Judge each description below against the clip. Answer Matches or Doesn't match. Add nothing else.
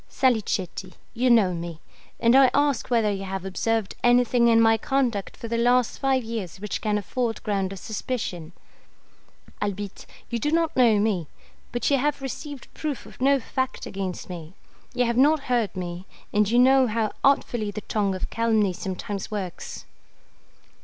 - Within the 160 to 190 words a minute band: Matches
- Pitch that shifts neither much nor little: Matches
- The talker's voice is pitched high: Matches